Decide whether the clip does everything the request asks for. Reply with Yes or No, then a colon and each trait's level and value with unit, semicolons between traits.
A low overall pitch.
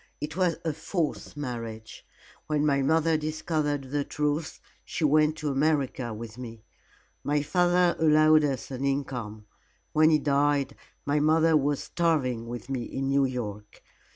No: medium, 145 Hz